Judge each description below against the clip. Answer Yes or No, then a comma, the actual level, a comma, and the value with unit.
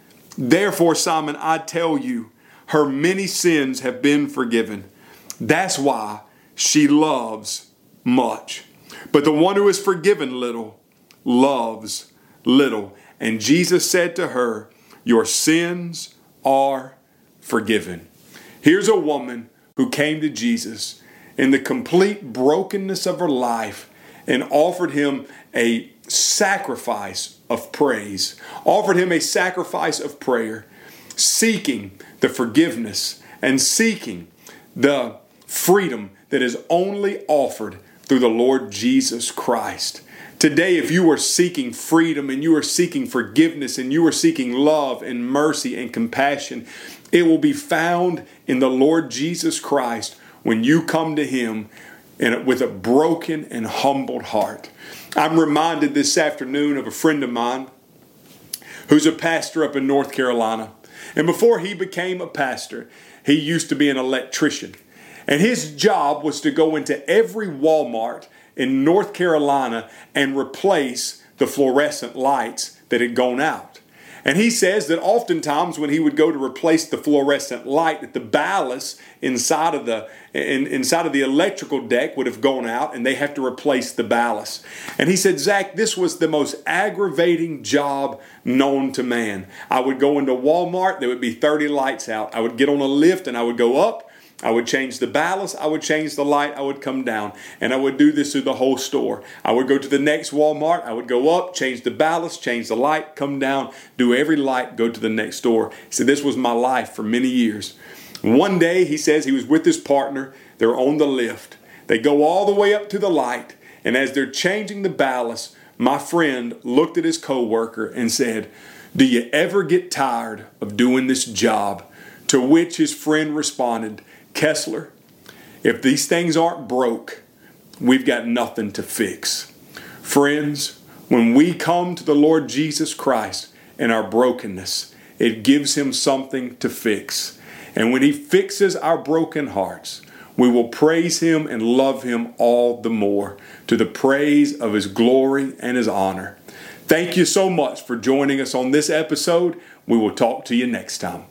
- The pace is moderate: Yes, average, 165 wpm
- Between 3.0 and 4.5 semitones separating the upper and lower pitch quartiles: No, average, 4.9 semitones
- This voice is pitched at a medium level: Yes, medium, 145 Hz